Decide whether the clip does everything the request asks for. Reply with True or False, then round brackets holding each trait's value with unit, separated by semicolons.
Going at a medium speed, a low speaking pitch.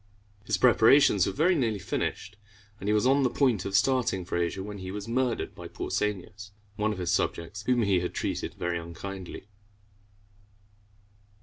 True (165 wpm; 105 Hz)